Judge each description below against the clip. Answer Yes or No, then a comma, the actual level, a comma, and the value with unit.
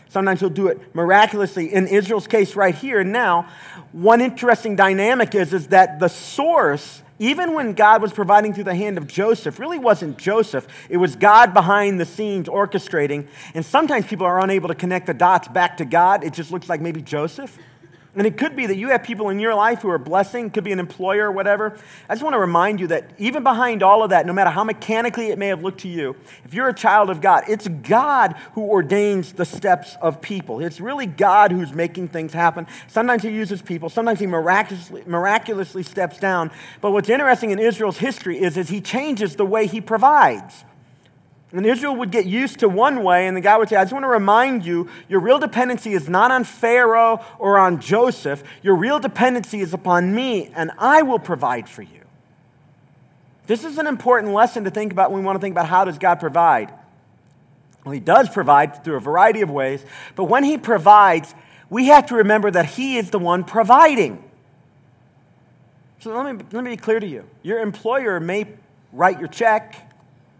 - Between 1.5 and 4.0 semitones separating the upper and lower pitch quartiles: No, average, 4.5 semitones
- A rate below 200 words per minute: No, fast, 205 wpm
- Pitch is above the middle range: Yes, high, 195 Hz